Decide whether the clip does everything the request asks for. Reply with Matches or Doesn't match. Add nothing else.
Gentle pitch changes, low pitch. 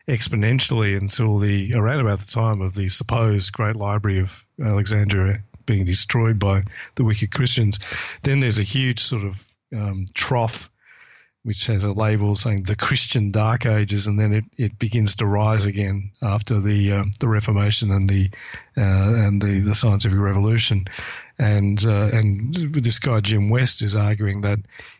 Matches